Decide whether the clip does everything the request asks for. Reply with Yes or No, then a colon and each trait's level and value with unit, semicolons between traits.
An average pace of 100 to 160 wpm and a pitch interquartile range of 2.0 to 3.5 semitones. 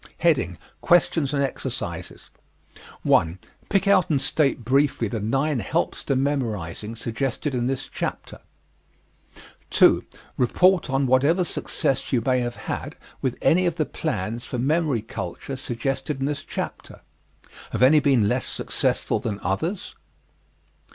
No: slow, 135 wpm; average, 4.2 semitones